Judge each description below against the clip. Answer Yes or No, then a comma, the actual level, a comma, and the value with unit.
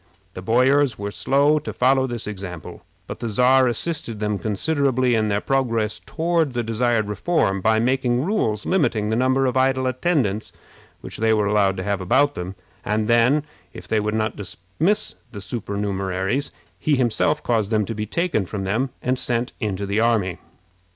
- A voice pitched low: Yes, low, 115 Hz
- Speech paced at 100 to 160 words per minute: No, average, 175 wpm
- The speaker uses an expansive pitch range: No, average, 4.2 semitones